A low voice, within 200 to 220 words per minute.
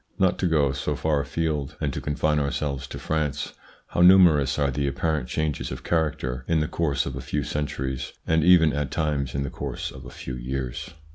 Yes: very low, 75 Hz; fast, 205 wpm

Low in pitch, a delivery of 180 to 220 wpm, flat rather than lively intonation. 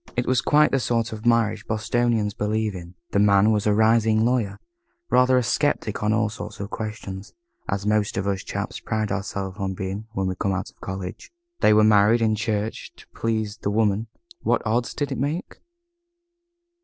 Yes: low, 110 Hz; average, 190 wpm; narrow, 2.3 semitones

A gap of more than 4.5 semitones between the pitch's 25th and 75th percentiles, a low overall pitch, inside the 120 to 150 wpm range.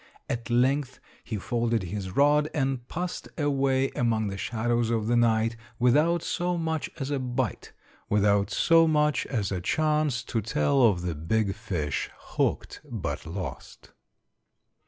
Yes: wide, 5.4 semitones; low, 120 Hz; average, 145 wpm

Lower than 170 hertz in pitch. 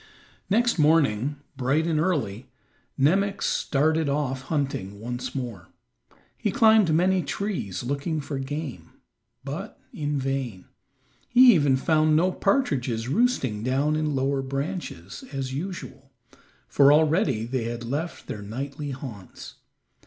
Yes: medium, 140 Hz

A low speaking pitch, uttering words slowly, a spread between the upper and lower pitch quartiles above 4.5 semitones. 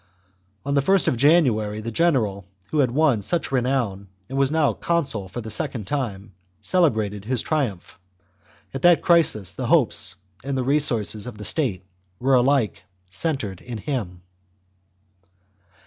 No: low, 125 Hz; average, 150 wpm; wide, 5.5 semitones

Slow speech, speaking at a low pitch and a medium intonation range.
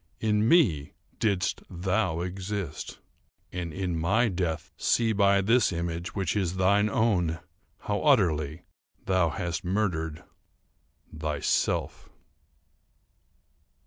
Yes: slow, 95 wpm; very low, 95 Hz; average, 3.6 semitones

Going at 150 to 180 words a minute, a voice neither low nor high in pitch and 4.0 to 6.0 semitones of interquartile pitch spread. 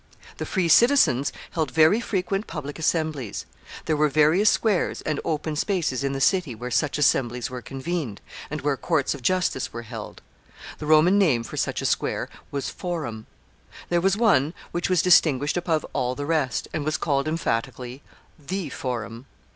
Yes: average, 170 wpm; medium, 150 Hz; average, 4.8 semitones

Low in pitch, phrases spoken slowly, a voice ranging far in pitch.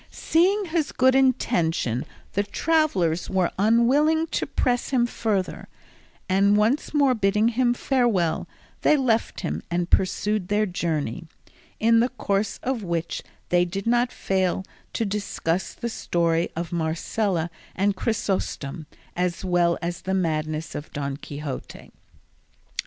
No: high, 195 Hz; slow, 130 wpm; wide, 5.8 semitones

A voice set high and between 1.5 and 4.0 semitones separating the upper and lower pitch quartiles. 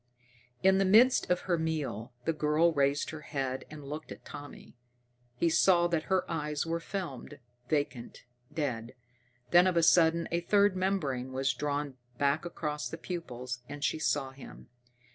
No: medium, 155 Hz; average, 3.6 semitones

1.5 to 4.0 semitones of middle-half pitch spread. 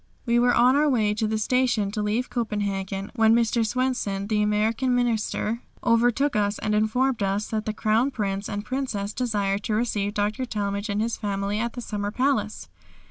Yes: average, 2.8 semitones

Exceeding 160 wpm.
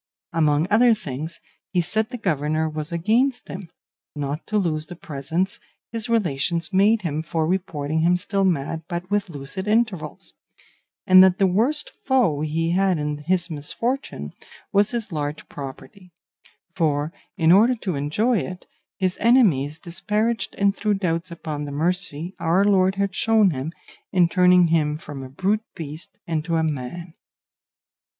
No: average, 155 wpm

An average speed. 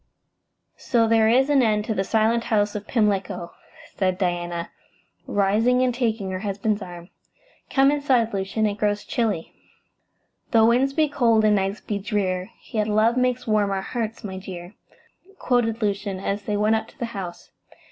Yes: average, 165 wpm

